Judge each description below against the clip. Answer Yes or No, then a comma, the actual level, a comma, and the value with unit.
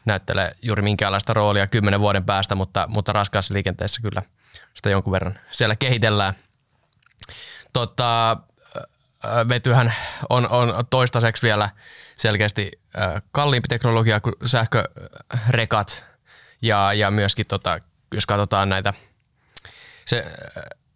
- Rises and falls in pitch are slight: No, average, 3.0 semitones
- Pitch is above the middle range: No, low, 105 Hz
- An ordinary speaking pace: Yes, average, 105 wpm